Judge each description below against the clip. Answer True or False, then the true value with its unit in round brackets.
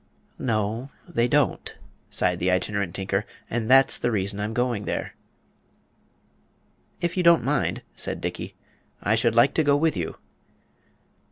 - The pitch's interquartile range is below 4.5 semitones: False (4.9 semitones)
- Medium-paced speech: True (145 wpm)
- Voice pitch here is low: True (115 Hz)